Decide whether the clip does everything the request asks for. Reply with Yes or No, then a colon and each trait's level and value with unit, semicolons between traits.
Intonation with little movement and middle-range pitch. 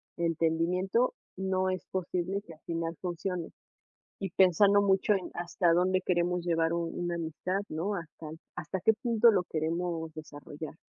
Yes: narrow, 2.3 semitones; medium, 175 Hz